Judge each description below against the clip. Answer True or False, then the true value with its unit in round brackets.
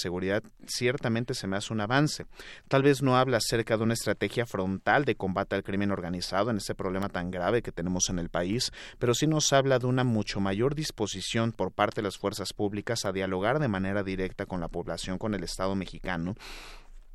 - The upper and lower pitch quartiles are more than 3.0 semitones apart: True (3.9 semitones)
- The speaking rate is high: True (205 wpm)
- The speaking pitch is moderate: False (100 Hz)